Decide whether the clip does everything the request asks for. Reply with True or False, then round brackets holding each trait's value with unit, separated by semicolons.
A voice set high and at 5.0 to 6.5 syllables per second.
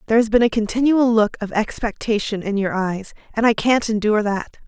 True (220 Hz; 5.8 syllables/s)